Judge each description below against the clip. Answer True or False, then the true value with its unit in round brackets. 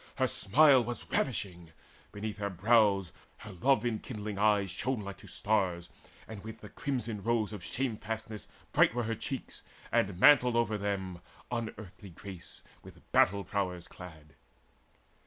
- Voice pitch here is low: True (105 Hz)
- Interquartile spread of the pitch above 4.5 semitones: False (3.5 semitones)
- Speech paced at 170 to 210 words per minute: False (140 wpm)